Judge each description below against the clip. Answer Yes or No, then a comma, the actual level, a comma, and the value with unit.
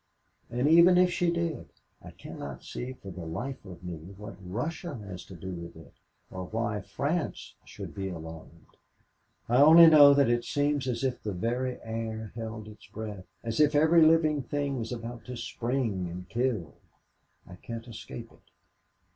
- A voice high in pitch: No, low, 115 Hz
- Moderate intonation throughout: No, wide, 6.9 semitones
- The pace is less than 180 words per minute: Yes, average, 170 wpm